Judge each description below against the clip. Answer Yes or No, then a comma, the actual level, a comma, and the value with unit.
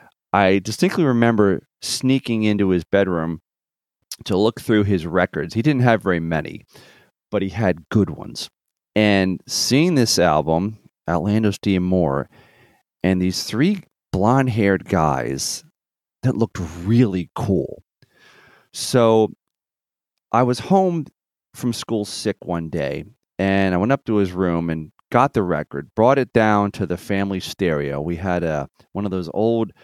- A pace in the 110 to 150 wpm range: Yes, average, 145 wpm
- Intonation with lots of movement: No, average, 4.2 semitones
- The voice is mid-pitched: No, low, 100 Hz